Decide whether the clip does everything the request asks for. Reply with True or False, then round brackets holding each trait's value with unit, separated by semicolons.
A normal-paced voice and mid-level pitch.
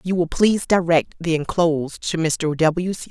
True (195 wpm; 170 Hz)